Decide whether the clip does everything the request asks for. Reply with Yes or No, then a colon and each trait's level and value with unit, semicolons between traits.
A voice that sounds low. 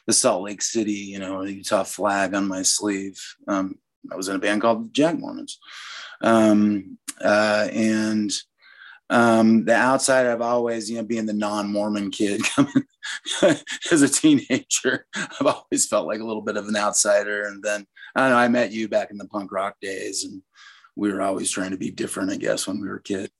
Yes: low, 110 Hz